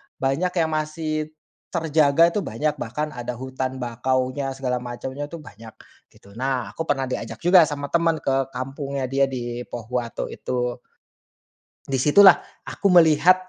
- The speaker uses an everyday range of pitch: Yes, average, 3.6 semitones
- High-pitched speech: No, low, 135 Hz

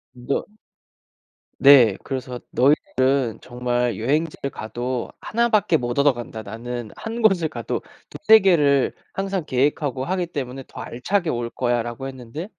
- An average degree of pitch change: Yes, average, 4.9 semitones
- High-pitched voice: No, low, 130 Hz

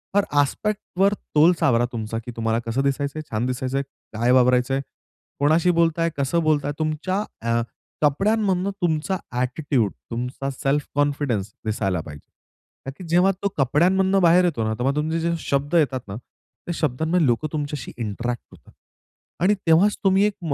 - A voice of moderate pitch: Yes, medium, 145 Hz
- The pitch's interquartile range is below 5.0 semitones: No, wide, 5.6 semitones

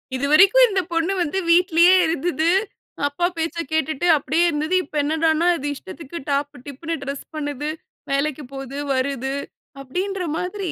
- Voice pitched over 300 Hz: Yes, very high, 315 Hz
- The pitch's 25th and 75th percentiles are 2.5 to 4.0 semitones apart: Yes, average, 3.7 semitones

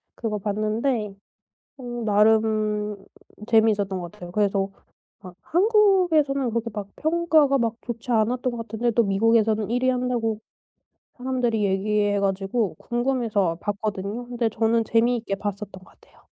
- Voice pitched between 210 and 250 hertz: Yes, high, 225 Hz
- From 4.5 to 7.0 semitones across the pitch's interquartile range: No, average, 3.0 semitones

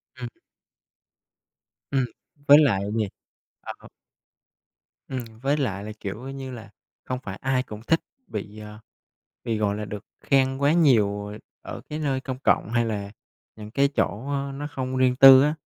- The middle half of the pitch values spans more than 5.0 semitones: No, average, 4.4 semitones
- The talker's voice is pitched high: No, low, 130 Hz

